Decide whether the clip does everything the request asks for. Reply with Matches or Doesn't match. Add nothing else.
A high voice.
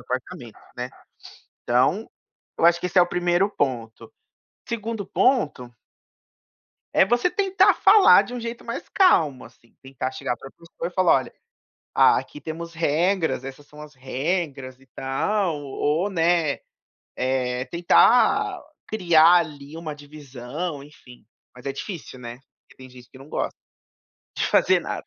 Doesn't match